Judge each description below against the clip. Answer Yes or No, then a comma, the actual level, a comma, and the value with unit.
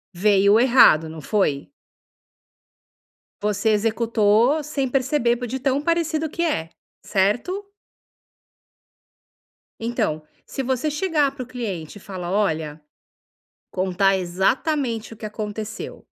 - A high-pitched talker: Yes, high, 225 Hz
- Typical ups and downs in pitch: No, wide, 5.7 semitones